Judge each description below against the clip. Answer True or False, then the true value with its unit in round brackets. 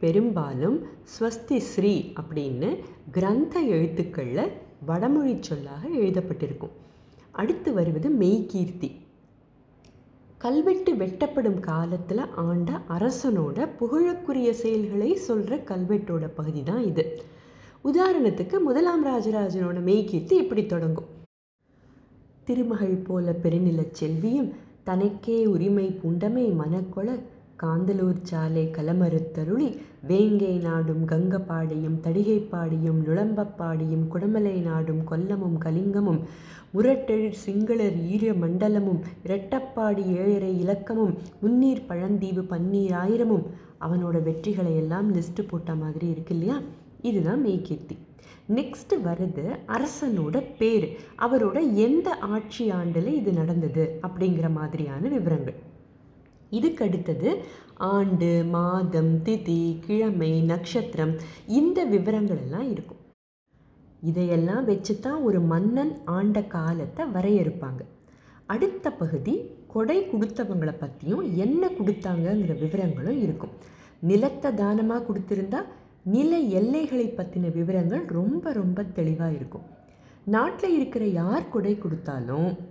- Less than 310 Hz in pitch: True (190 Hz)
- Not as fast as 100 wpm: True (90 wpm)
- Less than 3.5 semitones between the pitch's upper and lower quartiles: False (5.0 semitones)